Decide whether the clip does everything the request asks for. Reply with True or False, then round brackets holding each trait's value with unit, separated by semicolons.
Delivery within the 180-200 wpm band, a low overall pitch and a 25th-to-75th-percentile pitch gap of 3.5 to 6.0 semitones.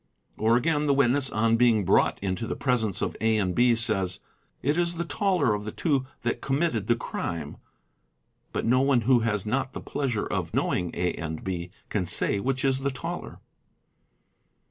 True (190 wpm; 120 Hz; 4.5 semitones)